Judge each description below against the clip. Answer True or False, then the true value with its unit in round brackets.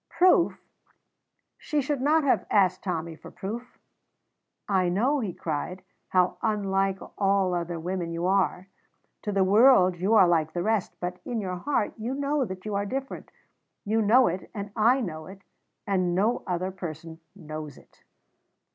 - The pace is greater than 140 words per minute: True (165 wpm)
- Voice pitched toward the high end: True (195 Hz)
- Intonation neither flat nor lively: True (3.9 semitones)